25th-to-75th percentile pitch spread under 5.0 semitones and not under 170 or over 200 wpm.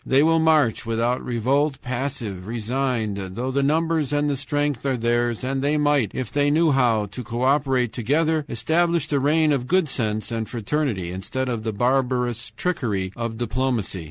Yes: average, 4.1 semitones; average, 175 wpm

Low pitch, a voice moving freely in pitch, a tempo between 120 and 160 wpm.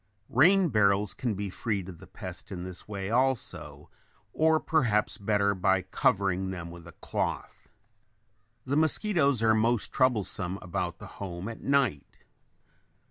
Yes: low, 100 Hz; wide, 5.7 semitones; average, 140 wpm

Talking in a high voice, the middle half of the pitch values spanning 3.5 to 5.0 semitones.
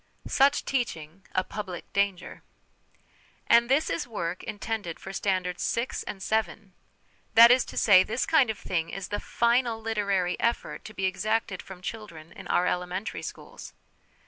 Yes: high, 200 Hz; average, 3.9 semitones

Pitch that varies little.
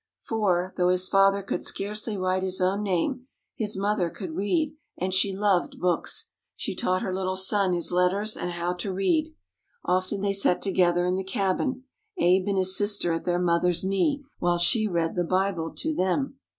Yes: narrow, 2.3 semitones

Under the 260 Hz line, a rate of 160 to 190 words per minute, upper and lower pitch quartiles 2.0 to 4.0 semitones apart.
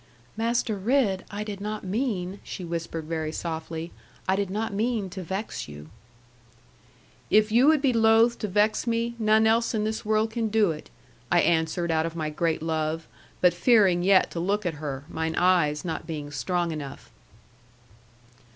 No: high, 190 Hz; average, 170 wpm; average, 5.0 semitones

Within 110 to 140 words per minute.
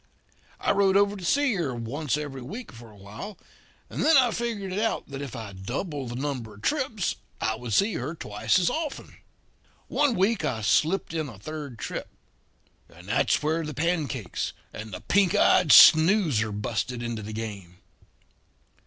No: average, 175 wpm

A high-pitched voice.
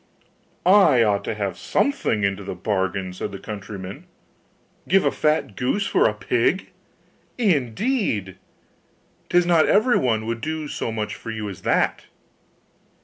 No: low, 110 Hz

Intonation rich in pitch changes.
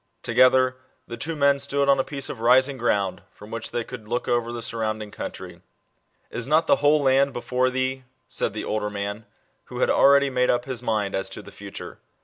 No: average, 3.4 semitones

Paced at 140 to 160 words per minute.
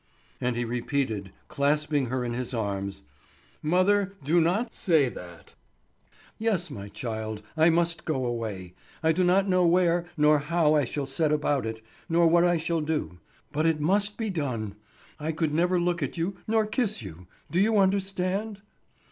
No: average, 170 wpm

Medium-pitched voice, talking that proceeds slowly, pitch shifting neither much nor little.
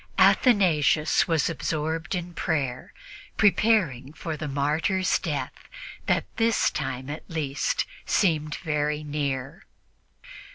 Yes: medium, 155 Hz; slow, 100 wpm; average, 3.3 semitones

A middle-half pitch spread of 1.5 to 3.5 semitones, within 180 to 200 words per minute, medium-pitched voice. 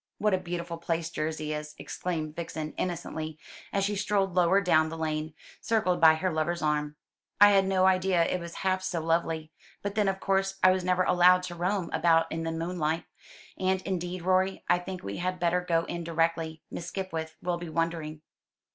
Yes: narrow, 2.5 semitones; average, 190 wpm; medium, 175 Hz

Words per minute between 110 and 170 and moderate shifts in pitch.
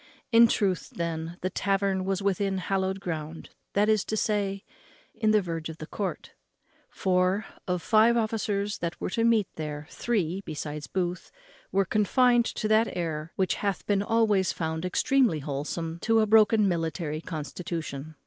Yes: average, 160 wpm; average, 4.5 semitones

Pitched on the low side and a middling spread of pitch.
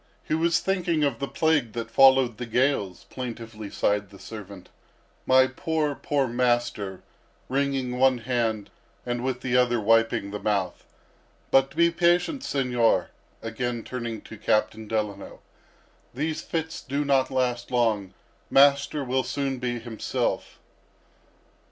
Yes: low, 125 Hz; average, 3.6 semitones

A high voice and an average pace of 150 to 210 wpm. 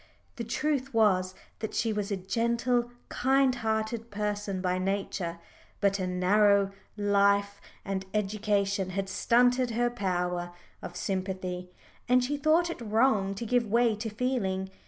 No: high, 205 Hz; average, 140 wpm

